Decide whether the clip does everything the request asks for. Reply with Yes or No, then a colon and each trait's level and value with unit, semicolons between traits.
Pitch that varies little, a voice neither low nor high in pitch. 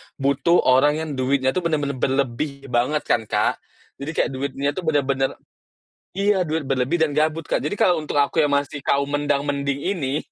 Yes: narrow, 2.3 semitones; medium, 145 Hz